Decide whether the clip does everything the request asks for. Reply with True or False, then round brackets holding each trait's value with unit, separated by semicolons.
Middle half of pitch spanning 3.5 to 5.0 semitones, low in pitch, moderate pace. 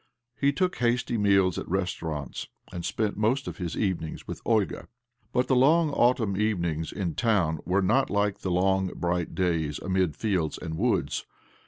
True (4.7 semitones; 95 Hz; 165 wpm)